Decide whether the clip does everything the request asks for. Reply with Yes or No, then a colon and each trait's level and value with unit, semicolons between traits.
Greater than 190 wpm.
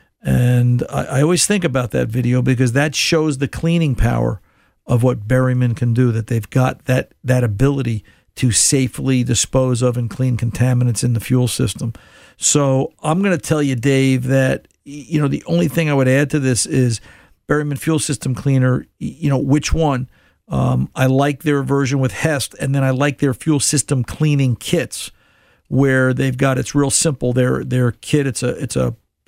No: average, 185 wpm